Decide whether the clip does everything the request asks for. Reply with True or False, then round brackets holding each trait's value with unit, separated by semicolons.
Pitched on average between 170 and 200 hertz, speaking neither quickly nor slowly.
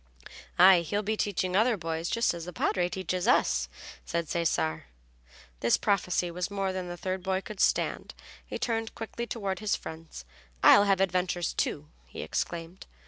True (185 Hz; 165 wpm)